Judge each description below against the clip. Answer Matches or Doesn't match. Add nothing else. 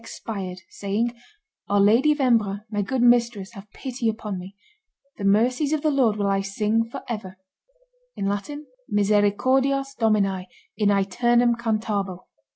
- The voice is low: Doesn't match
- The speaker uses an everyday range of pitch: Matches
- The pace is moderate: Doesn't match